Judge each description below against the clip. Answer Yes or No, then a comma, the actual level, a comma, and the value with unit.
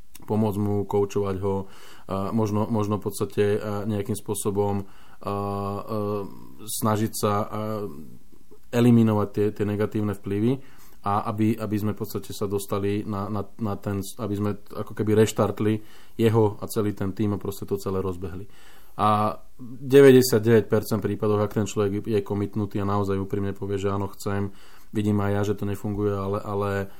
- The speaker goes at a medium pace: Yes, average, 150 wpm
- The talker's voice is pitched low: Yes, low, 105 Hz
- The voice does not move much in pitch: Yes, narrow, 1.2 semitones